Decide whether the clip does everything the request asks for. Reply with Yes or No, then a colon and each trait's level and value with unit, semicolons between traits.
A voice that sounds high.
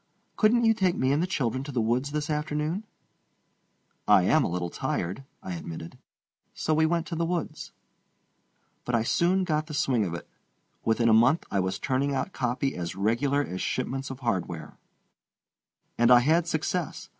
No: low, 135 Hz